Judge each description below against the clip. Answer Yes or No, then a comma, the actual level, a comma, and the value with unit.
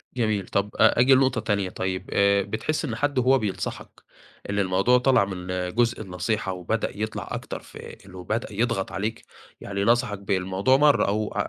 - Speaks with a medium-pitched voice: No, low, 105 Hz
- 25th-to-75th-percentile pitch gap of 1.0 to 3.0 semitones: No, average, 3.6 semitones